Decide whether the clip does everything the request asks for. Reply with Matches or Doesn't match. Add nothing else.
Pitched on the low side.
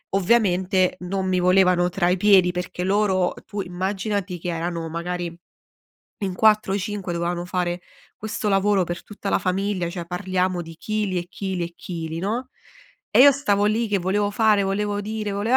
Doesn't match